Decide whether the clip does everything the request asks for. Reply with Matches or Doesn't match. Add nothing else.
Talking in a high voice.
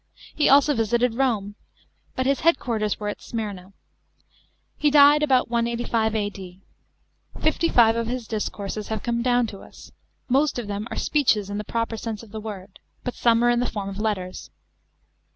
Matches